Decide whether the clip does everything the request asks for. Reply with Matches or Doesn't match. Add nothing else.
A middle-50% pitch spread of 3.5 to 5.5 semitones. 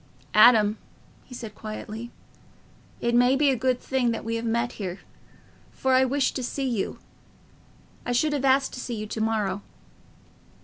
Doesn't match